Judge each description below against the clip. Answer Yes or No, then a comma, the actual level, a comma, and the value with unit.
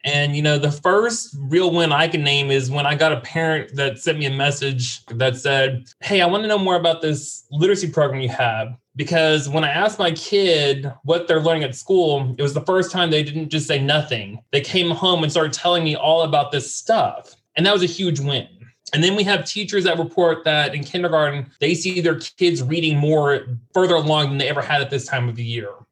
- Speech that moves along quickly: Yes, fast, 235 wpm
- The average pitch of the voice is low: No, medium, 155 Hz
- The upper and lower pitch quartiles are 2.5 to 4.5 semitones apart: Yes, average, 3.6 semitones